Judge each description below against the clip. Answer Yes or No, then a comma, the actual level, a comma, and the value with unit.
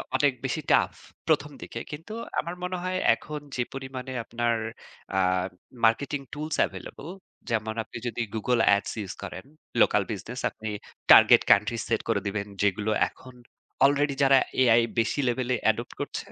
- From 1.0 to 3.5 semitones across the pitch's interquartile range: No, average, 4.4 semitones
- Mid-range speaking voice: No, low, 125 Hz